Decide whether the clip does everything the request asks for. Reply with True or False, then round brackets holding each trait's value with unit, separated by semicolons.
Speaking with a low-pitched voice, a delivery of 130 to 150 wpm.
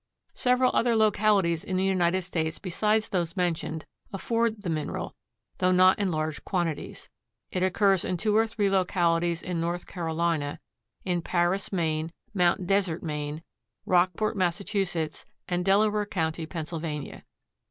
False (180 Hz; 135 wpm)